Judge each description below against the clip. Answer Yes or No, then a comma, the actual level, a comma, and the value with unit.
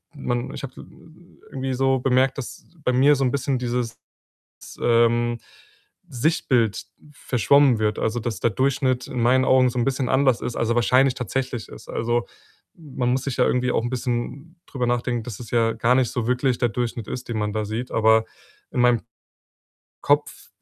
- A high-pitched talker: No, low, 125 Hz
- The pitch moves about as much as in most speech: No, narrow, 2.0 semitones